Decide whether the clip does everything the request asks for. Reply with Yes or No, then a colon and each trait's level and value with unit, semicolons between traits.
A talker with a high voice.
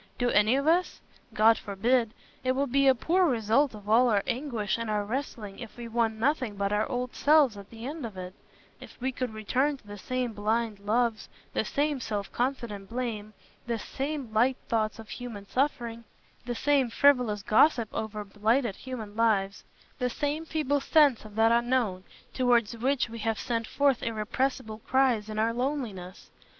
Yes: high, 235 Hz